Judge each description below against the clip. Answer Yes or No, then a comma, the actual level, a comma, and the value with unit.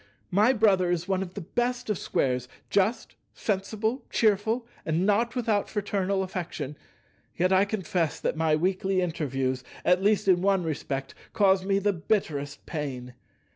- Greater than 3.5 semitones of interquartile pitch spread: Yes, average, 4.2 semitones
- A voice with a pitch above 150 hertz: Yes, high, 190 Hz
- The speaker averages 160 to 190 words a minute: No, average, 150 wpm